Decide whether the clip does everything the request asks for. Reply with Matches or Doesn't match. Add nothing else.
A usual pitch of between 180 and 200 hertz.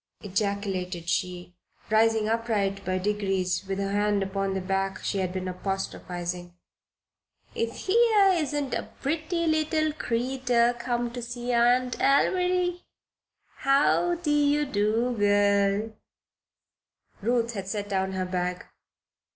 Doesn't match